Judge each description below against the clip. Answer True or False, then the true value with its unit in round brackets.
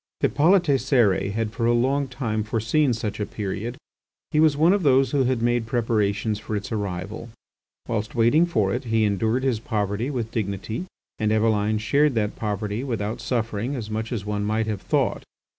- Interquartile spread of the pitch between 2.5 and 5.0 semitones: True (3.3 semitones)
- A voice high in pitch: False (115 Hz)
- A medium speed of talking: True (180 wpm)